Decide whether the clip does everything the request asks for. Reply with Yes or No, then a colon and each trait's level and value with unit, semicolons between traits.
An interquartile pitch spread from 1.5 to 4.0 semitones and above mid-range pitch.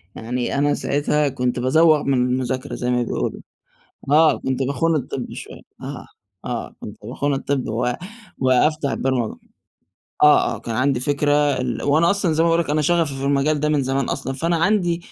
No: average, 3.1 semitones; medium, 140 Hz